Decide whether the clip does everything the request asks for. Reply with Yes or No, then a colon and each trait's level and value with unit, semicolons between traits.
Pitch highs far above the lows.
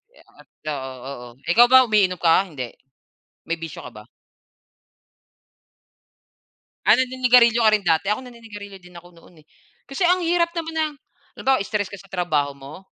Yes: wide, 7.3 semitones